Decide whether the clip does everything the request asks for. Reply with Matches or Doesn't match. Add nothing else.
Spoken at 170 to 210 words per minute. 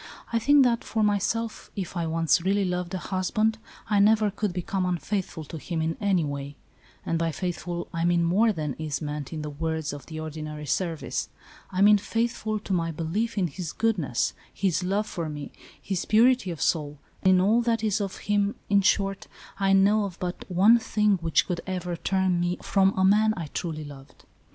Matches